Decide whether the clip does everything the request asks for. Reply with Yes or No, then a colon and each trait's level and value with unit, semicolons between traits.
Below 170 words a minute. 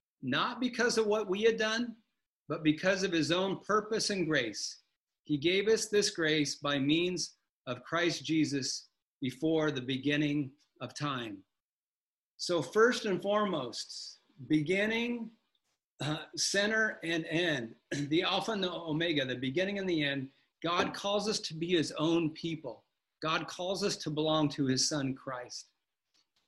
Yes: average, 150 wpm